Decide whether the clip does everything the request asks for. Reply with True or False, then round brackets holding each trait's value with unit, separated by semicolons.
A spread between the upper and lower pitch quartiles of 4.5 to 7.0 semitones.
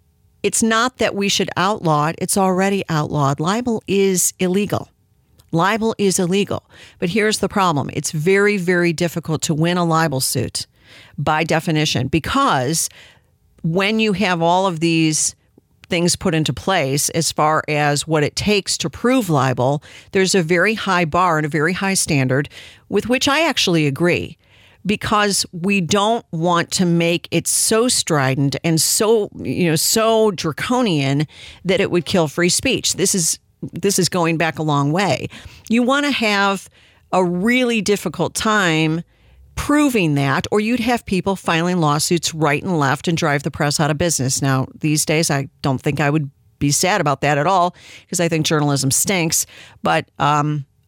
True (4.8 semitones)